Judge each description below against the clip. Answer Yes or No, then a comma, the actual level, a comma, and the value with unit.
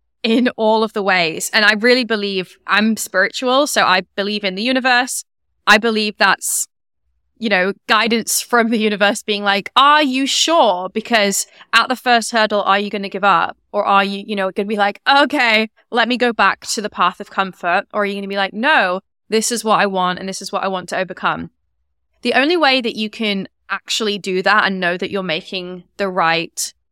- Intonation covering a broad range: No, average, 3.1 semitones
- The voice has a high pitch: Yes, high, 205 Hz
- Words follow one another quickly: Yes, fast, 220 wpm